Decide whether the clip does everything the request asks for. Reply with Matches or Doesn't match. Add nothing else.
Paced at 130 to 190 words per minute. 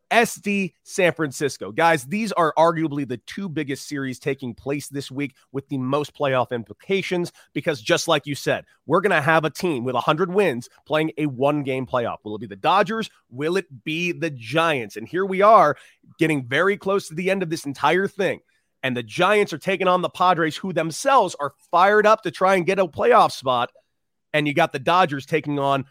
Doesn't match